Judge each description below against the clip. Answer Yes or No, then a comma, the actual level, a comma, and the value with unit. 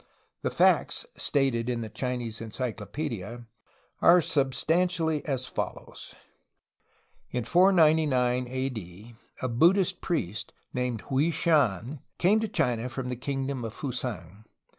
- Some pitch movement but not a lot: Yes, average, 4.9 semitones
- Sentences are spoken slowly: Yes, slow, 120 wpm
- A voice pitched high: No, low, 125 Hz